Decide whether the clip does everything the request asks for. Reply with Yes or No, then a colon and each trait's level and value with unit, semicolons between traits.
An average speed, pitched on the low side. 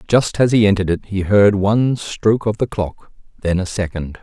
No: fast, 215 wpm; low, 100 Hz